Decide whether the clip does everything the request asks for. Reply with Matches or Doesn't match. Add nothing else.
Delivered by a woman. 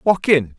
Doesn't match